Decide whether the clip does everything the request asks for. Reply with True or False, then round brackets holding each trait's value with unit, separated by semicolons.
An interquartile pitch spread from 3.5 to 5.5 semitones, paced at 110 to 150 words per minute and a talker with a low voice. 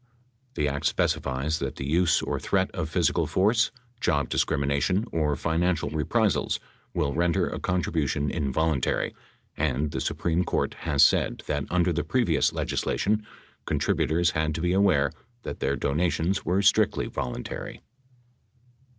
True (3.8 semitones; 135 wpm; 80 Hz)